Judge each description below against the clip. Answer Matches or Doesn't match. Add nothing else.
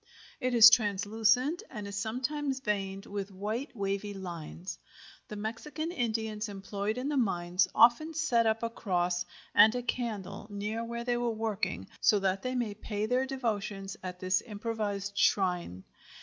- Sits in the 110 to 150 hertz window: Doesn't match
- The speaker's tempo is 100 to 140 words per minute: Doesn't match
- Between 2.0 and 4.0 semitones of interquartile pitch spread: Matches